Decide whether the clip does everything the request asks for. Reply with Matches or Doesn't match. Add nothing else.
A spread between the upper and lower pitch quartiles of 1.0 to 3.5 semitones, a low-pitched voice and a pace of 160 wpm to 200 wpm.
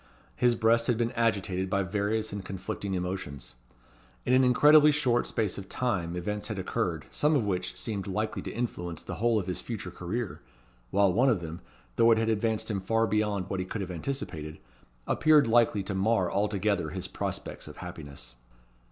Doesn't match